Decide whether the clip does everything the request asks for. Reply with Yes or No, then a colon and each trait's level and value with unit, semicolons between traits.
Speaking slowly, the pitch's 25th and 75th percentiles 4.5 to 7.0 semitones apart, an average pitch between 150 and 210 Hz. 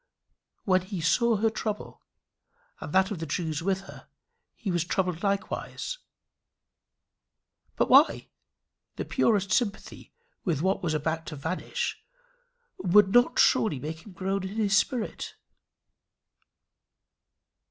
No: slow, 120 wpm; average, 3.9 semitones; high, 190 Hz